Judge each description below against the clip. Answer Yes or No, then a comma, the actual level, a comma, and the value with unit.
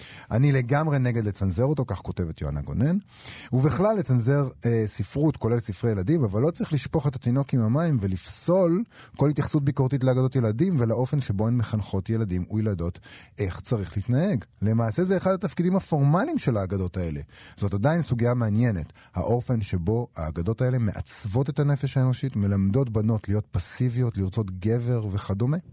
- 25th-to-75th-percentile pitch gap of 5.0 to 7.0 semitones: Yes, wide, 5.6 semitones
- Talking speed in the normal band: No, fast, 155 wpm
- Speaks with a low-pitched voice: Yes, low, 120 Hz